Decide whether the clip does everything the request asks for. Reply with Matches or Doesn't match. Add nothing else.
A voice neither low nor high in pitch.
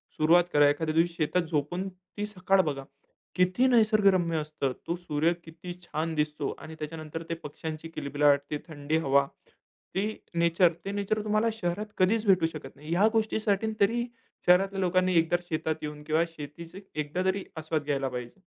Matches